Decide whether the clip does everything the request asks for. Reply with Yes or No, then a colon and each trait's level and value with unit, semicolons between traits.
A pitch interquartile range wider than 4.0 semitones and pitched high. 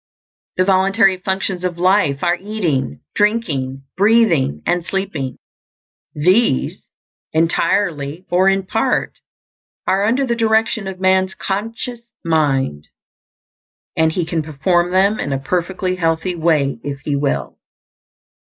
No: average, 4.4 semitones; medium, 180 Hz